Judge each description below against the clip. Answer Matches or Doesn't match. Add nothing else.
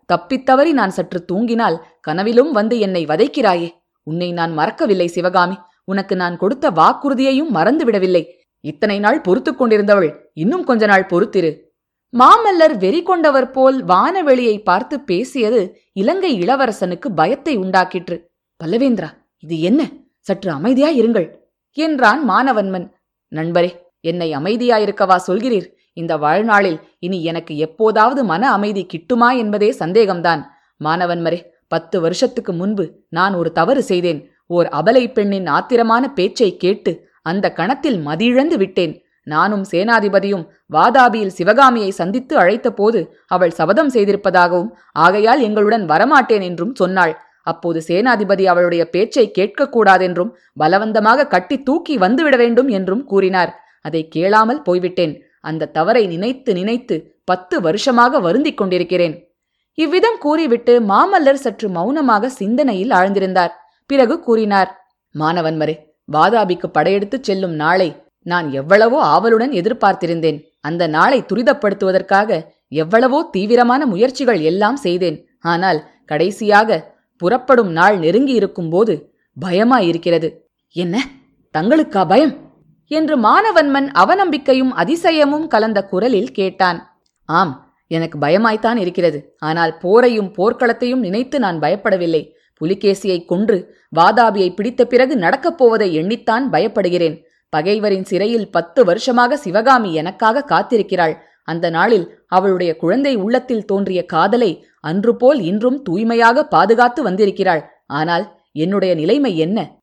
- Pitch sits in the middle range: Doesn't match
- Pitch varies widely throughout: Matches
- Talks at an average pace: Matches